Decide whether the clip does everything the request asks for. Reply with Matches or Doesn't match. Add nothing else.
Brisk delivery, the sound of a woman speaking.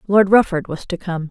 Matches